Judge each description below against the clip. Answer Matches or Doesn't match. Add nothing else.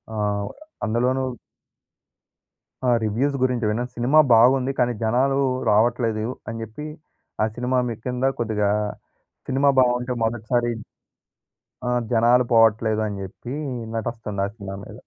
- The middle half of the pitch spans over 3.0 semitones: Doesn't match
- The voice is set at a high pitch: Doesn't match